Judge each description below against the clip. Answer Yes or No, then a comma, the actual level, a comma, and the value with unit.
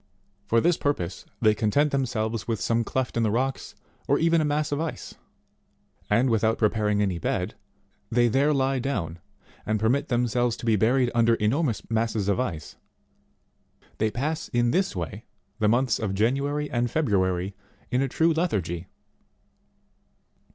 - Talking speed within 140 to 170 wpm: Yes, average, 160 wpm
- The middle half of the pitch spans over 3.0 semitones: Yes, average, 4.2 semitones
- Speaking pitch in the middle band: No, low, 115 Hz